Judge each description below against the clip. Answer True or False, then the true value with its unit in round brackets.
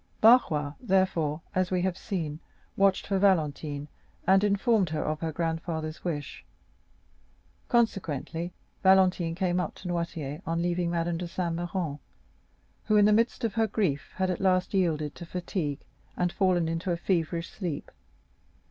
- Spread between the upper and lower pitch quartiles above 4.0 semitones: False (2.7 semitones)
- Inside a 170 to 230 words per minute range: False (150 wpm)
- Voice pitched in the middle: True (175 Hz)